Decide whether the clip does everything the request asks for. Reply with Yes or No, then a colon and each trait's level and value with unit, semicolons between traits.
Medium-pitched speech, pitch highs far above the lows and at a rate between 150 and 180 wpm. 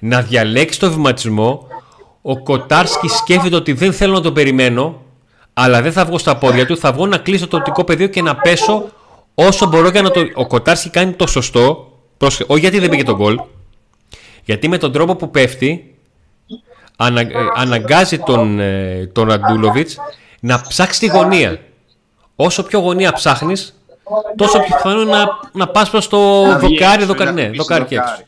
Yes: medium, 160 Hz; wide, 7.1 semitones; fast, 170 wpm